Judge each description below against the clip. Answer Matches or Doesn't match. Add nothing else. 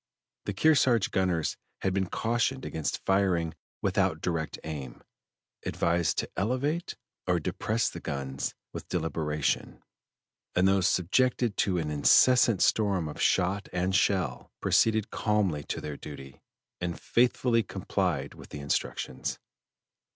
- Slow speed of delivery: Matches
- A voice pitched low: Matches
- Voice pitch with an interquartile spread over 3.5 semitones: Matches